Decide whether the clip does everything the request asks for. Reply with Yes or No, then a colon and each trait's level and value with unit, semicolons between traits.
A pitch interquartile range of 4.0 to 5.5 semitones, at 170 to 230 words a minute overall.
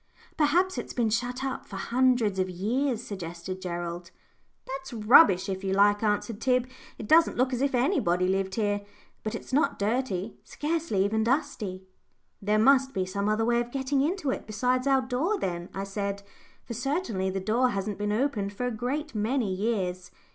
Yes: average, 5.1 semitones; average, 180 wpm